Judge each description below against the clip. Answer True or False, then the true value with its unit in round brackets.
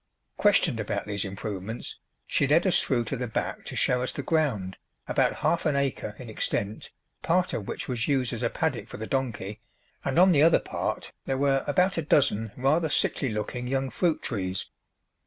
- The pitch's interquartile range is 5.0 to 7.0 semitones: True (5.4 semitones)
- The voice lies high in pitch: False (130 Hz)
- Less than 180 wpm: False (195 wpm)